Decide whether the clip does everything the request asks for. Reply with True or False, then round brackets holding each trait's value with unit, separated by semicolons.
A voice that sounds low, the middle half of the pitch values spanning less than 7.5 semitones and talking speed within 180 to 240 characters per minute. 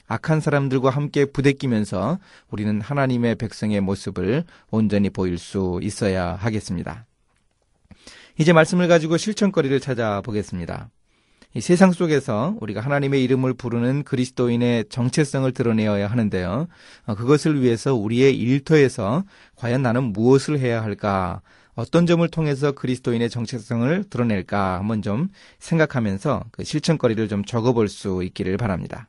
False (120 Hz; 5.3 semitones; 350 characters per minute)